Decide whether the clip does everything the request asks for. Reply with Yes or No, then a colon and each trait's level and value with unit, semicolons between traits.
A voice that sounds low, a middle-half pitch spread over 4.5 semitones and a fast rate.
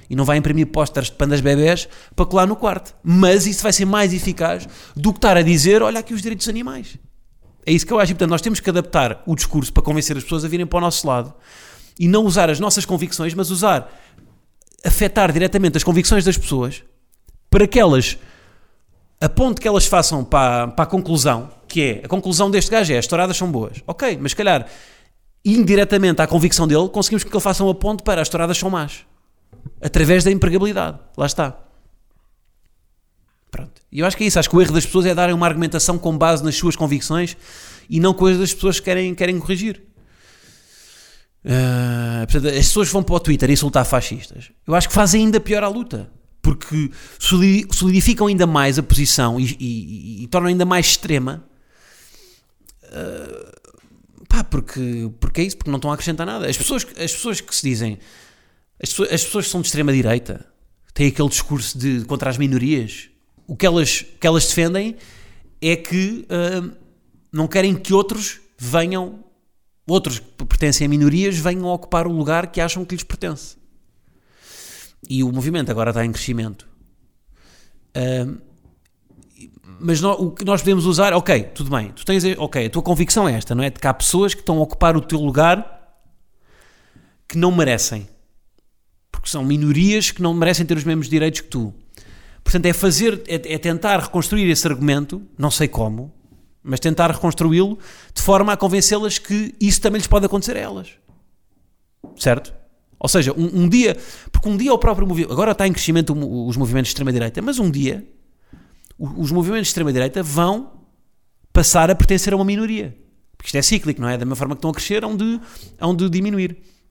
No: medium, 170 Hz; wide, 5.4 semitones; fast, 190 wpm